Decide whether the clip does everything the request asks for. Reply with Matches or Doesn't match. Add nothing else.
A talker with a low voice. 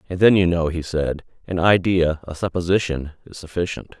Matches